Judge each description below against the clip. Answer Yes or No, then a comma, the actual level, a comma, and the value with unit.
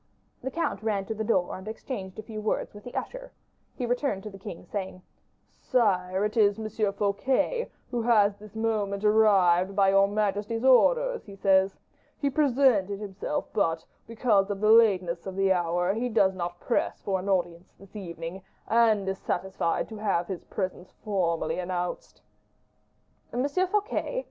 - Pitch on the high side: Yes, high, 205 Hz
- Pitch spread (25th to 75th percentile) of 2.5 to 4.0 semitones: Yes, average, 3.1 semitones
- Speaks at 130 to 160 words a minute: No, average, 170 wpm